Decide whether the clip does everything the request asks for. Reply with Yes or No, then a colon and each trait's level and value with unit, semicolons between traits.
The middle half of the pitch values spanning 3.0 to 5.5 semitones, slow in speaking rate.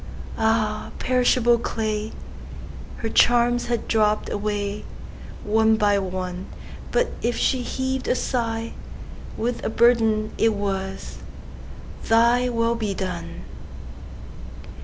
No: narrow, 2.4 semitones; slow, 85 wpm